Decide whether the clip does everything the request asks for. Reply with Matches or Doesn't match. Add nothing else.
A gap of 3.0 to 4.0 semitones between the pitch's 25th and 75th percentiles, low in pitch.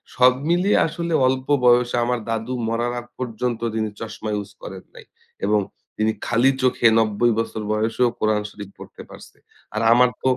Doesn't match